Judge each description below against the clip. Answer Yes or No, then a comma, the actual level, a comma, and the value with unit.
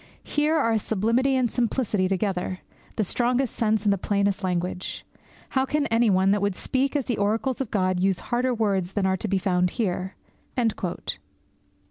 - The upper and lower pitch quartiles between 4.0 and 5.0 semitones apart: Yes, average, 4.4 semitones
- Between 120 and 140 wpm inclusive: No, average, 170 wpm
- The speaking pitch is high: Yes, high, 210 Hz